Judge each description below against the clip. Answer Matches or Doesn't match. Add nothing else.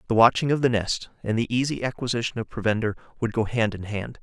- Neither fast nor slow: Doesn't match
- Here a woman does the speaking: Doesn't match